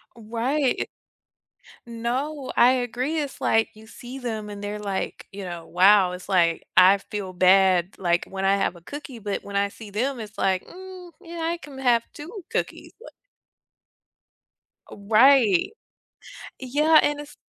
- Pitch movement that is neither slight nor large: No, wide, 5.9 semitones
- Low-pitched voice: No, high, 220 Hz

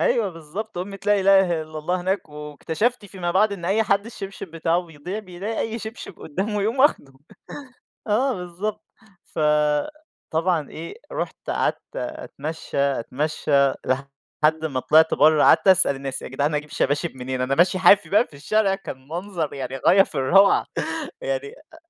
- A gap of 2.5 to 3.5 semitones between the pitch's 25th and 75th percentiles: No, average, 5.3 semitones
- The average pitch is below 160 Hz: No, medium, 175 Hz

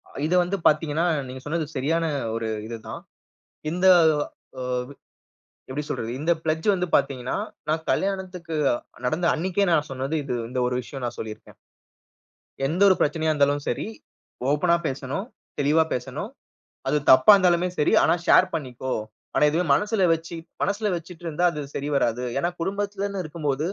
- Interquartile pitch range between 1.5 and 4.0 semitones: No, average, 4.6 semitones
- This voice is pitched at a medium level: Yes, medium, 155 Hz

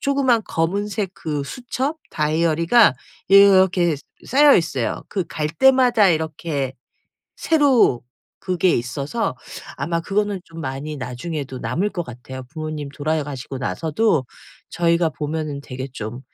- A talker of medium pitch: Yes, medium, 165 Hz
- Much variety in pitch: Yes, wide, 6.1 semitones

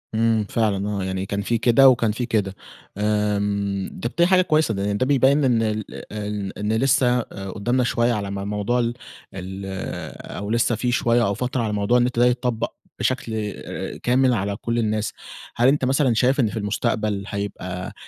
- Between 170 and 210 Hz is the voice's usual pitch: No, low, 110 Hz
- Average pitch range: Yes, average, 3.3 semitones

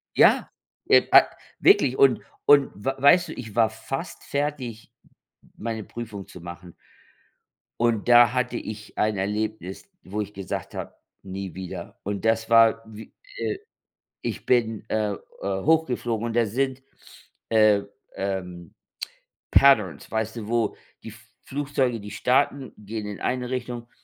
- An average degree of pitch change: Yes, average, 3.3 semitones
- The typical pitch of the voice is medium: No, low, 110 Hz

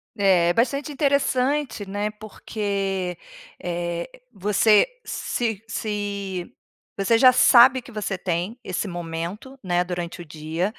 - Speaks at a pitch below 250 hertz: Yes, high, 200 Hz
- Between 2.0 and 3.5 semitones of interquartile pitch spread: No, average, 4.5 semitones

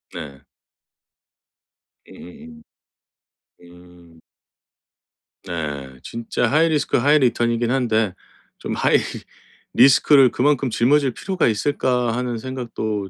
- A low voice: Yes, low, 120 Hz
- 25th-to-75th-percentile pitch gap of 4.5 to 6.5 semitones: No, wide, 7.0 semitones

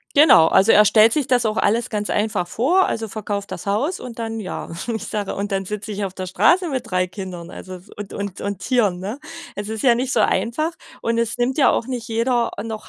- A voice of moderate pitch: No, high, 215 Hz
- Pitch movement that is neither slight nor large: Yes, average, 3.1 semitones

